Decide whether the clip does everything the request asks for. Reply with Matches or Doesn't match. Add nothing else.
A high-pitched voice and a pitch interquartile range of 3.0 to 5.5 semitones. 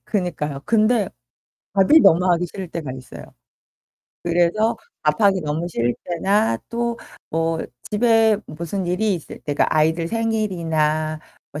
Doesn't match